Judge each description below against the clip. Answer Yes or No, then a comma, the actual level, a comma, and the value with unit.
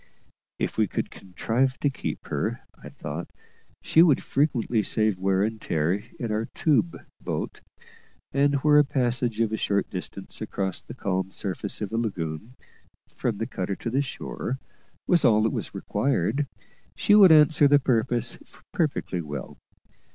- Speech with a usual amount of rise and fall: No, wide, 6.0 semitones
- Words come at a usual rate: Yes, average, 160 wpm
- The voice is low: Yes, low, 115 Hz